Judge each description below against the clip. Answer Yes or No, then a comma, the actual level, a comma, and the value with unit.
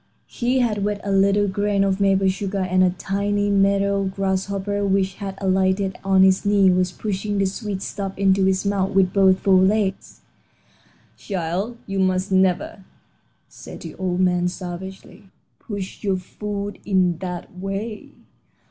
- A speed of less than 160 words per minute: Yes, average, 150 wpm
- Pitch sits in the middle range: No, high, 195 Hz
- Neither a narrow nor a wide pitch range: No, narrow, 1.2 semitones